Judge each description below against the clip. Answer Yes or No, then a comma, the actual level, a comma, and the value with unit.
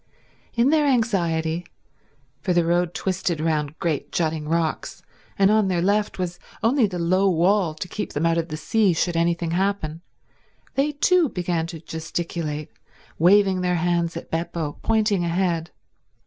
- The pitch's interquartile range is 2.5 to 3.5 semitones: Yes, average, 3.2 semitones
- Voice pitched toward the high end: No, medium, 175 Hz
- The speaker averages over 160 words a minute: No, average, 155 wpm